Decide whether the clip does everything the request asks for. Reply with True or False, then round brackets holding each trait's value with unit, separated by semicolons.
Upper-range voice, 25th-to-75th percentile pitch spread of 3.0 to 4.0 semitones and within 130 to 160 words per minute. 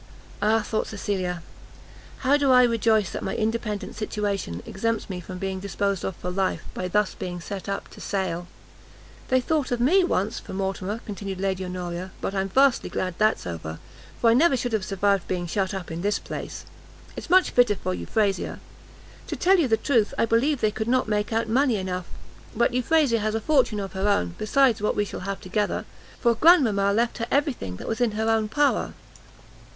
False (210 Hz; 3.7 semitones; 200 wpm)